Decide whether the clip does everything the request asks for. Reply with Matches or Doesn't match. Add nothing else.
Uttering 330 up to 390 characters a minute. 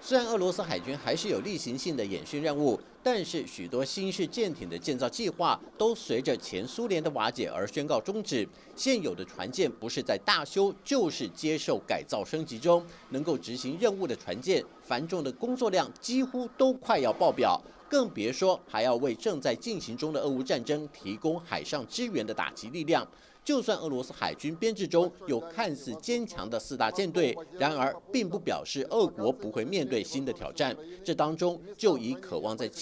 Doesn't match